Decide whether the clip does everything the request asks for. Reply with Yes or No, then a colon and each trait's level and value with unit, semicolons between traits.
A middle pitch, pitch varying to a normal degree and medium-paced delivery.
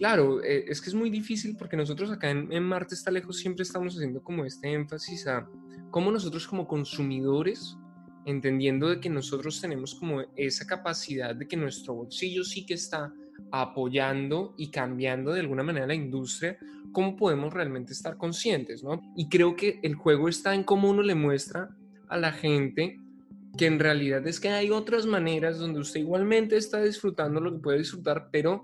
Yes: medium, 160 Hz; average, 4.8 semitones; average, 180 wpm